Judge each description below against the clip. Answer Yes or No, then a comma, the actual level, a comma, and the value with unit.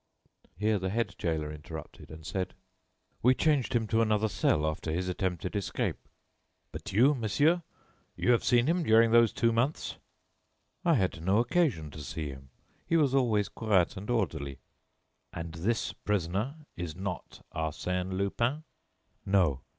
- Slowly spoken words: No, average, 150 wpm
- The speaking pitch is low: Yes, low, 100 Hz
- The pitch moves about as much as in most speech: No, wide, 5.9 semitones